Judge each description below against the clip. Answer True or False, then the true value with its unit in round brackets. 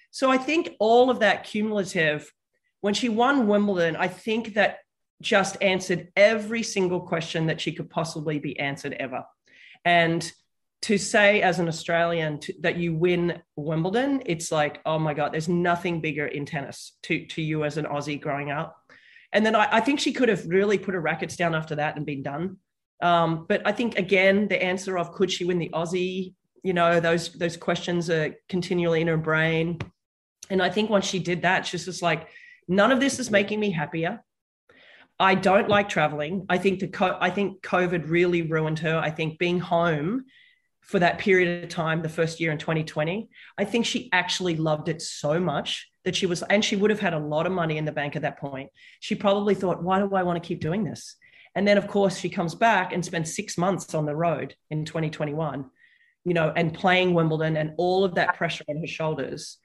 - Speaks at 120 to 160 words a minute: False (205 wpm)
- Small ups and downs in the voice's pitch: False (3.7 semitones)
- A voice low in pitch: False (175 Hz)